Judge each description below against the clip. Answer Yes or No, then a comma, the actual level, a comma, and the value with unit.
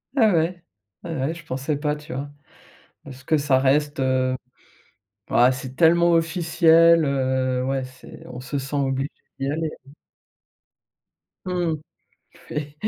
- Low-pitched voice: No, medium, 145 Hz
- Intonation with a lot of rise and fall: No, average, 3.7 semitones